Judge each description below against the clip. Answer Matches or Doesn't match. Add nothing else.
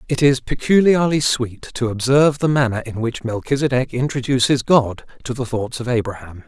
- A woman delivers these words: Doesn't match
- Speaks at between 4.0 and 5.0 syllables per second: Doesn't match